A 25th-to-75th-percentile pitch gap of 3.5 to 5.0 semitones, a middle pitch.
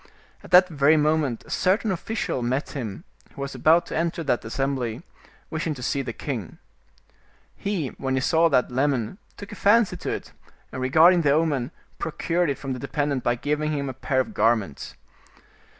Yes: average, 4.2 semitones; medium, 145 Hz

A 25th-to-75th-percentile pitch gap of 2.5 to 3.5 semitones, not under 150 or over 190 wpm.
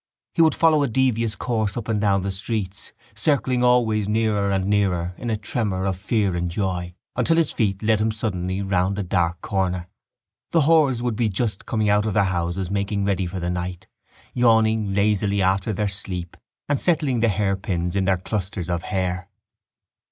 Yes: average, 3.2 semitones; average, 185 wpm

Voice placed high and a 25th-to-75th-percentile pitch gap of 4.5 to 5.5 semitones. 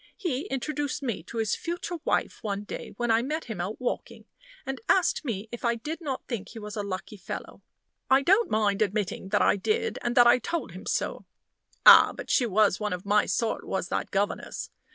Yes: high, 230 Hz; average, 4.8 semitones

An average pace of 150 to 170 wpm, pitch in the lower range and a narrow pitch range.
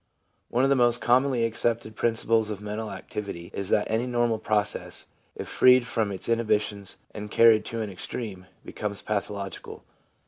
Yes: average, 160 wpm; low, 110 Hz; narrow, 2.2 semitones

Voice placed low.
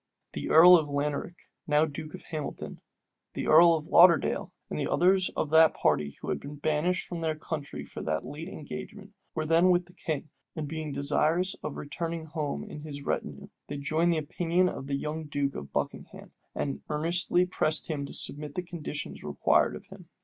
No: medium, 155 Hz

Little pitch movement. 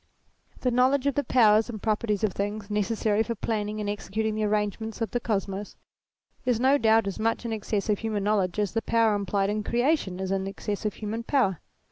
Yes: narrow, 1.9 semitones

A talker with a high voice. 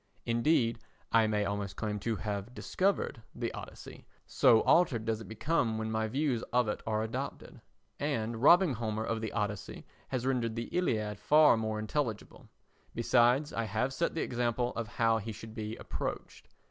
No: low, 115 Hz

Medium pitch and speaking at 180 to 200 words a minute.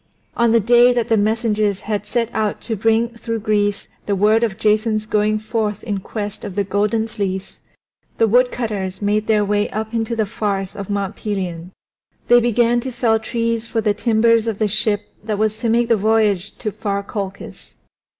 No: high, 215 Hz; average, 190 wpm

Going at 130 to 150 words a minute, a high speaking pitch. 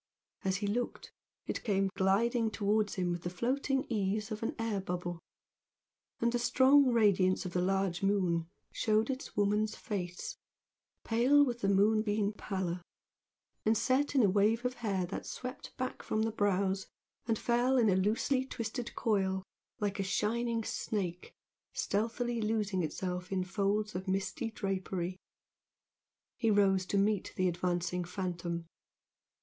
Yes: average, 145 wpm; high, 205 Hz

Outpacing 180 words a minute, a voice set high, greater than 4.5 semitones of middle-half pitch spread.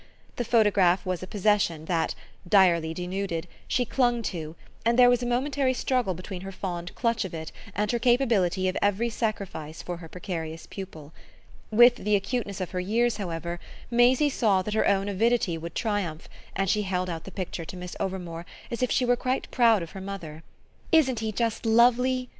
Yes: average, 190 wpm; high, 200 Hz; average, 5.1 semitones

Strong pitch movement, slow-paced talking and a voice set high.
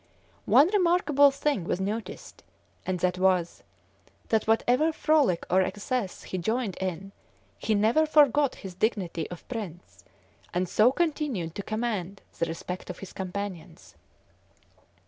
Yes: wide, 6.1 semitones; slow, 130 wpm; high, 205 Hz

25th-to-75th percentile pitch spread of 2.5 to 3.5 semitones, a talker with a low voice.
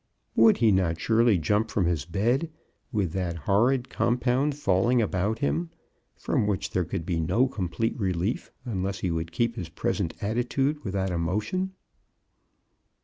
No: average, 5.3 semitones; low, 100 Hz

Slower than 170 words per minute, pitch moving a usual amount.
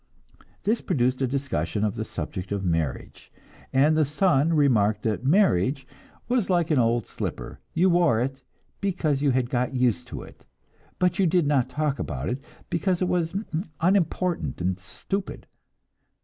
No: average, 160 wpm; wide, 6.4 semitones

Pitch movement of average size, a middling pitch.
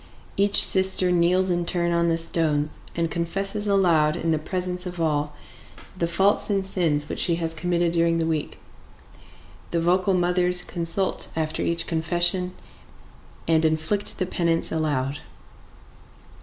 No: narrow, 2.0 semitones; medium, 170 Hz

